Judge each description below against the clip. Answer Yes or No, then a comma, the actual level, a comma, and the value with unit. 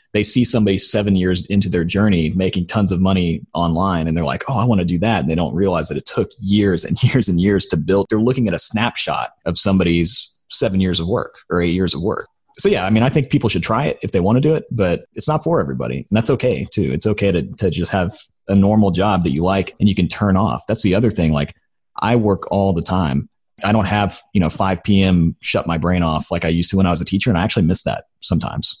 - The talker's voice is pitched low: Yes, very low, 95 Hz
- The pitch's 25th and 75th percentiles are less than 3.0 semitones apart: No, average, 3.5 semitones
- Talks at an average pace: No, fast, 270 wpm